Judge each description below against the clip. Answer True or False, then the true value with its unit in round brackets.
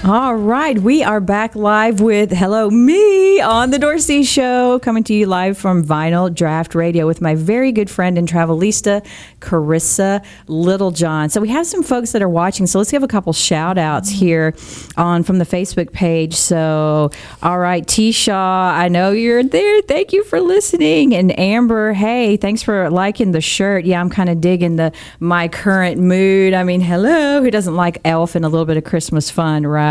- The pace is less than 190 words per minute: False (195 wpm)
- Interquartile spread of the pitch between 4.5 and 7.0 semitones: True (4.8 semitones)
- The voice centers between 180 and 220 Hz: True (190 Hz)